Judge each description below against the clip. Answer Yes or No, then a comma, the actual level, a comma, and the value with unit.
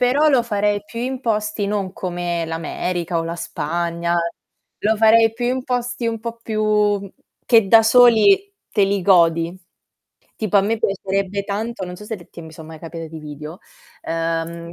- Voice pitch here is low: No, high, 200 Hz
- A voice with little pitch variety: No, average, 4.9 semitones